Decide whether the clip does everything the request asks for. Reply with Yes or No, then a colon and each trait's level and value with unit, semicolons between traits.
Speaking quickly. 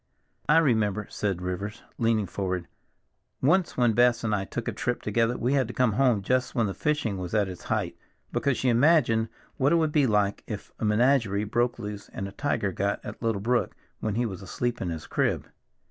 Yes: fast, 210 wpm